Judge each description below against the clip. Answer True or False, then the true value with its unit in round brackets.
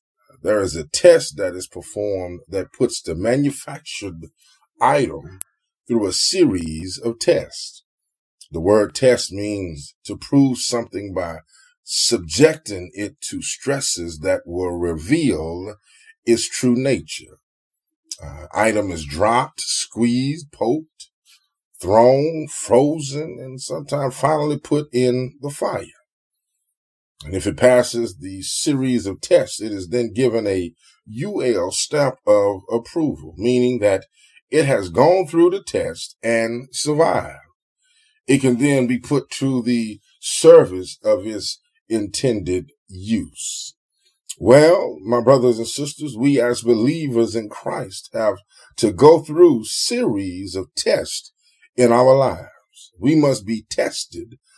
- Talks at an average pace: False (125 wpm)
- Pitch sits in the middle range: False (125 Hz)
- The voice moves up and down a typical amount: False (6.5 semitones)